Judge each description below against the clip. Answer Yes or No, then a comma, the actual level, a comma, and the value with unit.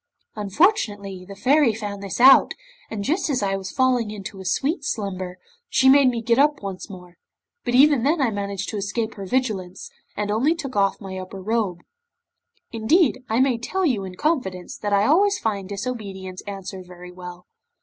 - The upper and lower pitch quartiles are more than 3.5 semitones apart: Yes, average, 5.1 semitones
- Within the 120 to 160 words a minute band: No, average, 180 wpm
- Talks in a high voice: Yes, high, 210 Hz